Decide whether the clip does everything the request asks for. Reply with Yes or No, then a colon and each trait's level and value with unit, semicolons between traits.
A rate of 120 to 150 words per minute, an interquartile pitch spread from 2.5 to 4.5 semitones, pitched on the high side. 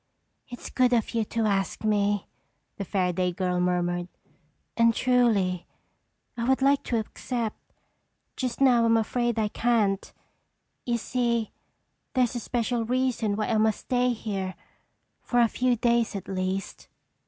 Yes: average, 140 wpm; average, 3.6 semitones; high, 225 Hz